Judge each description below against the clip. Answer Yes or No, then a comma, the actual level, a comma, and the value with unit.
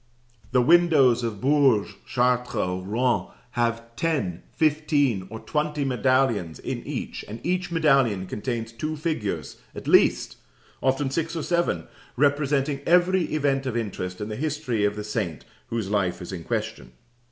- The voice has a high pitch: No, low, 125 Hz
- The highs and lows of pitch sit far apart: Yes, wide, 6.0 semitones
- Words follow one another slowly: No, average, 150 wpm